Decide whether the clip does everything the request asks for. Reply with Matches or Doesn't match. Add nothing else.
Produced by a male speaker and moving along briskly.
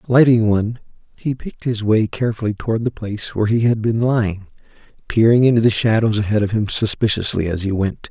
Doesn't match